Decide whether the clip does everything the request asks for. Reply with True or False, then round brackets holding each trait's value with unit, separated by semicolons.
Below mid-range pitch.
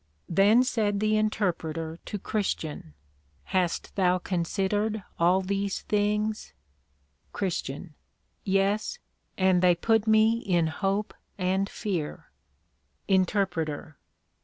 False (195 Hz)